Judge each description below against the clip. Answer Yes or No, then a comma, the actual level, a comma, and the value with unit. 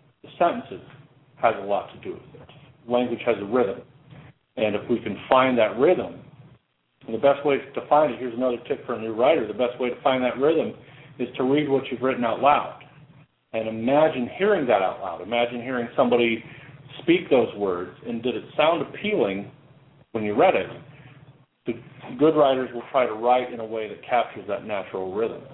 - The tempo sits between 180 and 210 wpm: Yes, average, 200 wpm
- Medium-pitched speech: No, low, 125 Hz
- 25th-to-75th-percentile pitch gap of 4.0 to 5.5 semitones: No, average, 3.0 semitones